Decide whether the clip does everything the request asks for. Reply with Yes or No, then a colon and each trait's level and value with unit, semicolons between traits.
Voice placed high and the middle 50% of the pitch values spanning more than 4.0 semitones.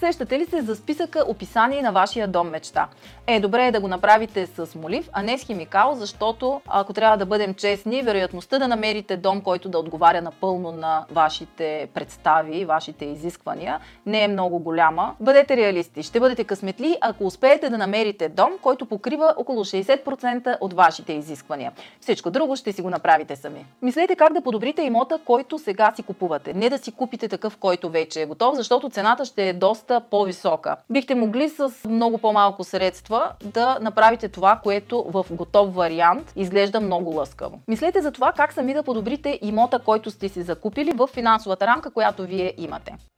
Yes: high, 215 Hz; average, 5.3 semitones